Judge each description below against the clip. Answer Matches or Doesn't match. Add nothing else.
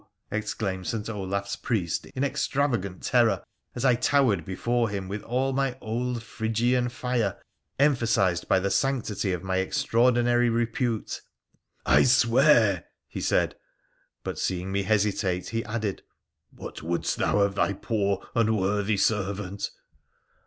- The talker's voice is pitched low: Matches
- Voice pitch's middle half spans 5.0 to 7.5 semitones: Doesn't match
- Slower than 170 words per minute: Matches